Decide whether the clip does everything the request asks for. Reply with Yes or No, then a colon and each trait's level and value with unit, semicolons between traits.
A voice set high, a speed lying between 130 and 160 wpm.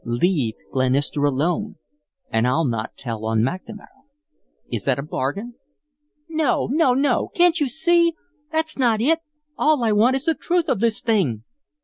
Yes: high, 215 Hz; average, 155 wpm